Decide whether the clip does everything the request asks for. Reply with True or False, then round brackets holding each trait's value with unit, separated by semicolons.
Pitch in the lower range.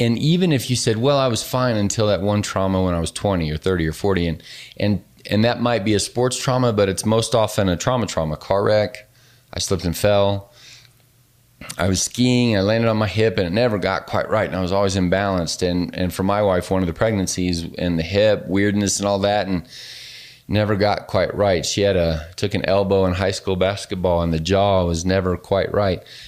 True (100 Hz)